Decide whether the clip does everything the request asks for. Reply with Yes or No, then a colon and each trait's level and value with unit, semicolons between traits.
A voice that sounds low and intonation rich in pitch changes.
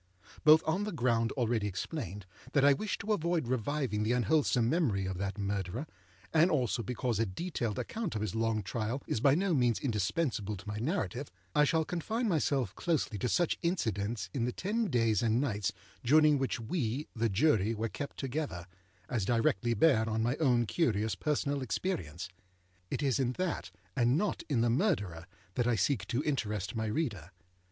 Yes: low, 120 Hz; wide, 5.9 semitones